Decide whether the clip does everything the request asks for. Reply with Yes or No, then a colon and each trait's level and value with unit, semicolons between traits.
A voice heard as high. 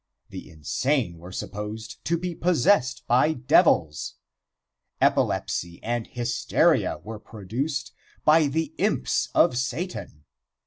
No: low, 120 Hz